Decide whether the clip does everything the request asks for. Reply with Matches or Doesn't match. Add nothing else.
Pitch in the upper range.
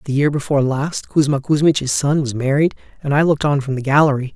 Doesn't match